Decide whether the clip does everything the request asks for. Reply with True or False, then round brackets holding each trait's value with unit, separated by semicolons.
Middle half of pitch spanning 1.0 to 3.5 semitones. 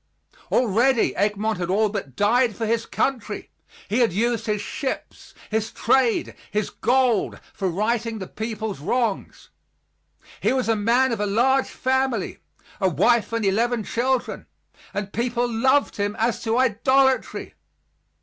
True (3.0 semitones)